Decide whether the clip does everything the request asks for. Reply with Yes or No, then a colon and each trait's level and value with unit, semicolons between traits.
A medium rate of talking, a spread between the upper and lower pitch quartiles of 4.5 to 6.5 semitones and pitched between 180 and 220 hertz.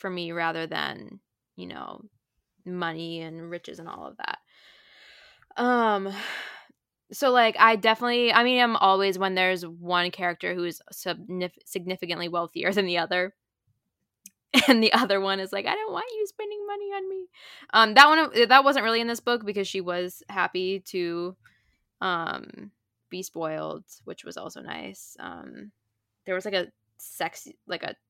Yes: average, 165 wpm; average, 5.2 semitones; high, 190 Hz